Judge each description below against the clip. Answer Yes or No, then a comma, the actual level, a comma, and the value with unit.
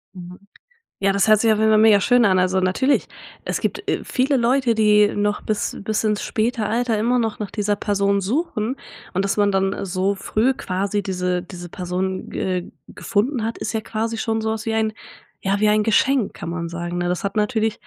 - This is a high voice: Yes, high, 210 Hz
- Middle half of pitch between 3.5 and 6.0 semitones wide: No, average, 2.7 semitones